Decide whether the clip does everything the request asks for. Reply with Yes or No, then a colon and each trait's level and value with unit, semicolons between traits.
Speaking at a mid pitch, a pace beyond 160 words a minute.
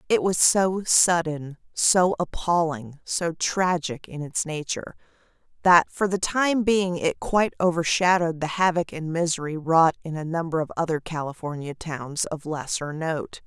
No: medium, 165 Hz; average, 150 wpm